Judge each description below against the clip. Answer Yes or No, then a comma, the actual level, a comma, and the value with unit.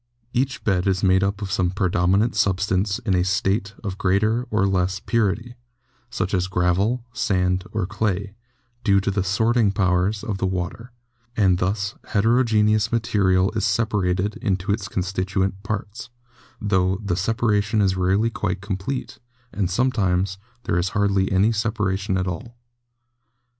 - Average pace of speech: Yes, average, 145 wpm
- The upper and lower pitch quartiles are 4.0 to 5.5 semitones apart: No, narrow, 2.4 semitones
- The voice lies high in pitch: No, low, 100 Hz